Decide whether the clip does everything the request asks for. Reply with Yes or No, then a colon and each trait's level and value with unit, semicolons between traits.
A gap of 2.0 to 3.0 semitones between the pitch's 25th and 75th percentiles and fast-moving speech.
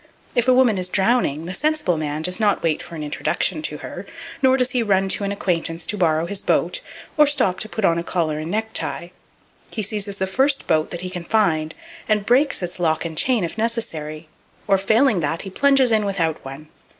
No: average, 5.3 semitones; fast, 215 wpm